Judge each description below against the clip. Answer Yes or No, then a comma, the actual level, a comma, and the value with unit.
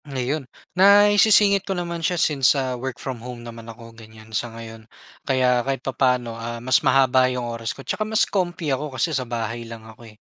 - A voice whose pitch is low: Yes, low, 130 Hz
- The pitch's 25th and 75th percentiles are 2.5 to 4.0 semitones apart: No, average, 4.6 semitones